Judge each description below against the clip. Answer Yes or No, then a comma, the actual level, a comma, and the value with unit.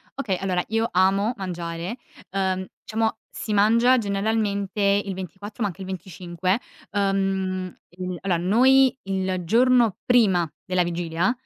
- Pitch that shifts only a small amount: No, average, 3.0 semitones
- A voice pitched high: Yes, high, 195 Hz